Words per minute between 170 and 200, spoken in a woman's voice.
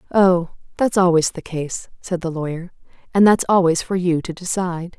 Yes: average, 180 wpm; female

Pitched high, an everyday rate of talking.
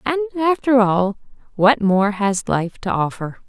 Yes: high, 220 Hz; average, 155 wpm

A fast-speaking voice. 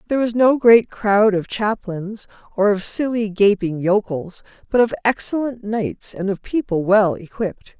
No: average, 160 wpm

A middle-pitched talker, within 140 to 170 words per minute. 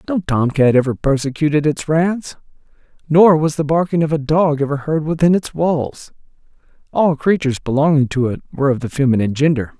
No: medium, 150 Hz; average, 180 wpm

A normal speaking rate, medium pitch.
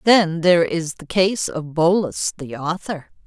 Yes: average, 165 wpm; medium, 170 Hz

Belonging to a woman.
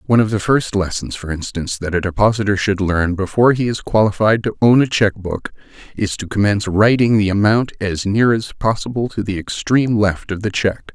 No: male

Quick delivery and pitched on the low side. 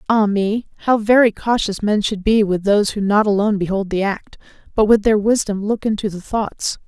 No: fast, 210 wpm; high, 210 Hz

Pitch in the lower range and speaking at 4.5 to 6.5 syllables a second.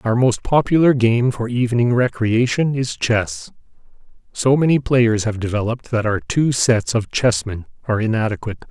Yes: low, 120 Hz; 5.1 syllables/s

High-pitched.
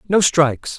No: medium, 160 Hz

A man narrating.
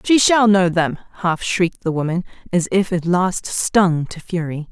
No: female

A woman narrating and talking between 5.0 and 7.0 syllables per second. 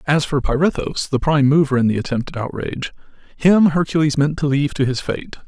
No: male; 6.0 syllables/s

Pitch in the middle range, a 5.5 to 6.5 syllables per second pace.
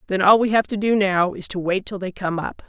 No: high, 195 Hz; 5.7 syllables/s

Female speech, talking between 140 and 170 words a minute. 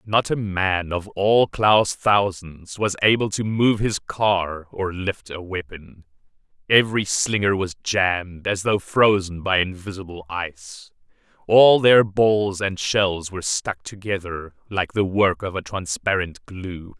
No: male; average, 150 wpm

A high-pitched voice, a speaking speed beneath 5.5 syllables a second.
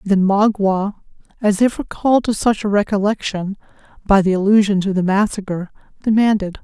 Yes: high, 200 Hz; 5.3 syllables/s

